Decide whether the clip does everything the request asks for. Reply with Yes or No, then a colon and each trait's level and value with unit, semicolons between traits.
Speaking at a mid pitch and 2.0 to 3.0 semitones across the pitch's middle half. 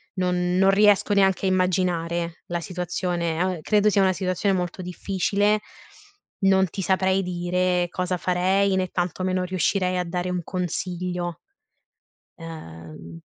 No: medium, 180 Hz; narrow, 1.3 semitones